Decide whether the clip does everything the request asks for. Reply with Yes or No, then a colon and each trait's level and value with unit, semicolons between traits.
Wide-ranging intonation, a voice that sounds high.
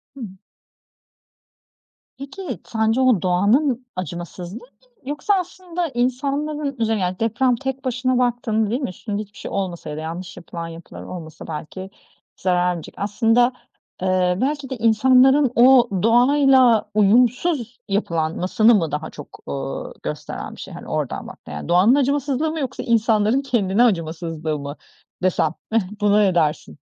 Yes: wide, 6.4 semitones; high, 225 Hz